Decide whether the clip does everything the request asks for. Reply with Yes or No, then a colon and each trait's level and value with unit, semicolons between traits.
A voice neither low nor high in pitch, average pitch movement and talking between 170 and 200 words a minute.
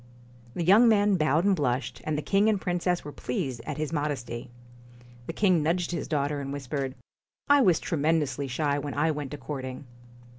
Yes: medium, 150 Hz; average, 4.0 semitones; average, 185 wpm